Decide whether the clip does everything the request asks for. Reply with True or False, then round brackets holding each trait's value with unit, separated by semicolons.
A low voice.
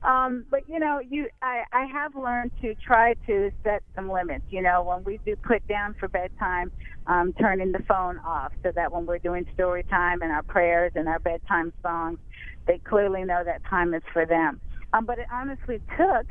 False (195 Hz)